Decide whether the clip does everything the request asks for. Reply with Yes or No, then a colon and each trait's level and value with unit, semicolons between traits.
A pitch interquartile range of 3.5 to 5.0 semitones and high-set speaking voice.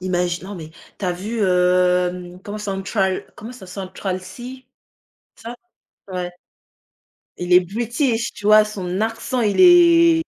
Yes: average, 4.1 semitones; high, 195 Hz